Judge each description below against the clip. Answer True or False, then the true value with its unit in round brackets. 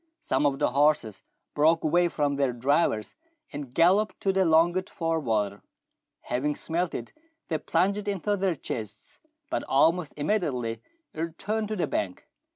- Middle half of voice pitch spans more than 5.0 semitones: True (5.5 semitones)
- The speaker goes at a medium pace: True (160 wpm)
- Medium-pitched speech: True (155 Hz)